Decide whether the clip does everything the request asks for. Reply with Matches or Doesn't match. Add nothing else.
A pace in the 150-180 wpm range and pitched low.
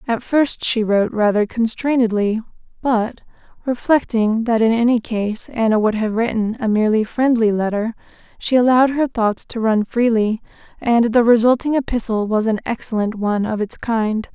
Doesn't match